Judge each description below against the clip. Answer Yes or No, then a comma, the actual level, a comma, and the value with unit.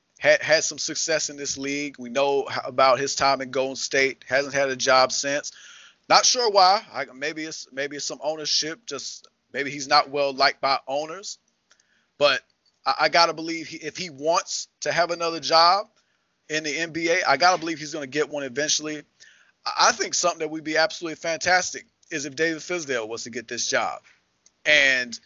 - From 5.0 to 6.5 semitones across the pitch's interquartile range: No, average, 2.8 semitones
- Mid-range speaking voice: Yes, medium, 150 Hz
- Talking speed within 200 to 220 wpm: No, average, 190 wpm